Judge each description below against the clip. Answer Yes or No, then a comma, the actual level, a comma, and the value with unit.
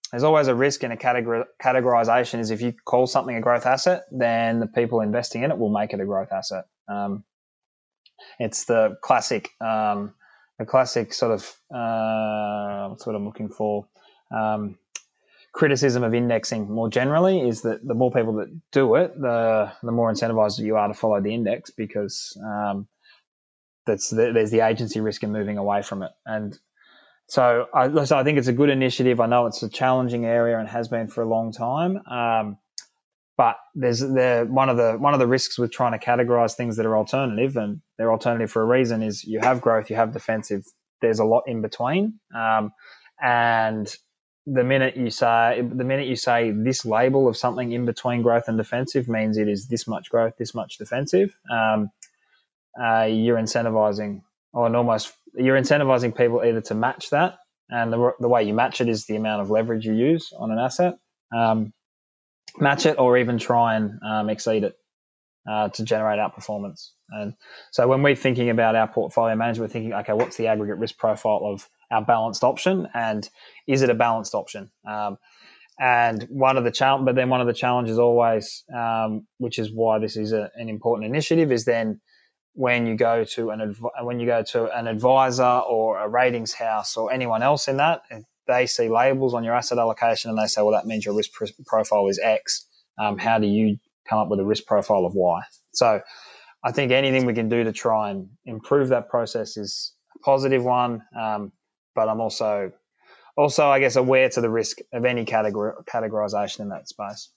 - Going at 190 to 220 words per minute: Yes, average, 195 wpm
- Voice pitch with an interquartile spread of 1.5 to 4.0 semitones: Yes, narrow, 2.6 semitones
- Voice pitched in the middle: No, low, 115 Hz